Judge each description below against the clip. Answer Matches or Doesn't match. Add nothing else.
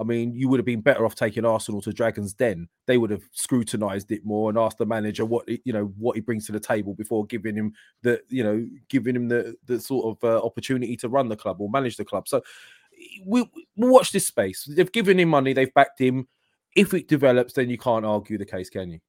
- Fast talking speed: Matches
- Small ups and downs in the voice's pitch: Doesn't match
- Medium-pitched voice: Doesn't match